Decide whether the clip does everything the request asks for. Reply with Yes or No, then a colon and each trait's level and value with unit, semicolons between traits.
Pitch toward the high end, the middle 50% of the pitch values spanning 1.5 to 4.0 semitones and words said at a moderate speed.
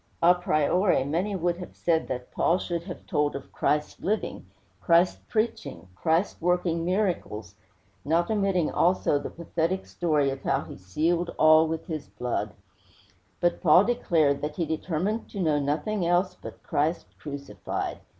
No: medium, 170 Hz; average, 3.3 semitones; average, 150 wpm